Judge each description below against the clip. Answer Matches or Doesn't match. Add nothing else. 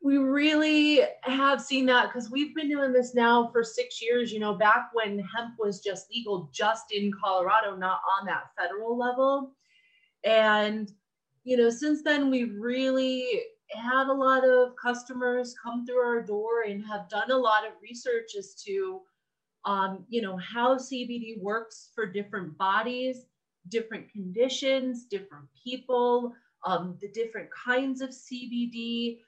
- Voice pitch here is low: Doesn't match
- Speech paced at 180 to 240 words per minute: Doesn't match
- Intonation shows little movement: Doesn't match